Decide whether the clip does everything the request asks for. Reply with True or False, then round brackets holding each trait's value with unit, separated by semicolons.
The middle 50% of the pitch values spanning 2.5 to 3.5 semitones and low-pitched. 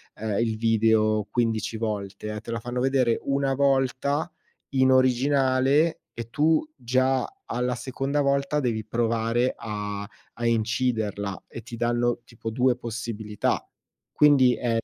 True (2.9 semitones; 120 Hz)